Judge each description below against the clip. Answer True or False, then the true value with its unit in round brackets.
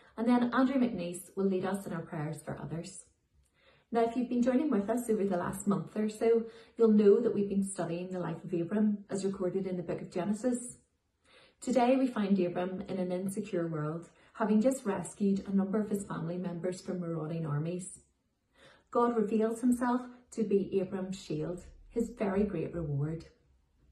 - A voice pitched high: True (195 Hz)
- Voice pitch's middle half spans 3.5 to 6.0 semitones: True (4.4 semitones)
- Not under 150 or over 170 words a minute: False (185 wpm)